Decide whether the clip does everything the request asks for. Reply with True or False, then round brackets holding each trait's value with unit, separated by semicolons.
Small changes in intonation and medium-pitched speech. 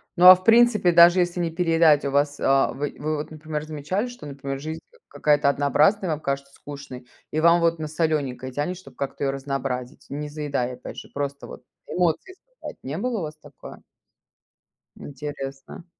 False (3.4 semitones; 150 Hz)